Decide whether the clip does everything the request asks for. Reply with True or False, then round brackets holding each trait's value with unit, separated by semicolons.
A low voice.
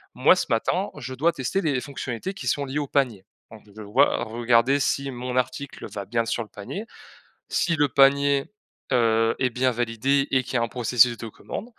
True (125 Hz)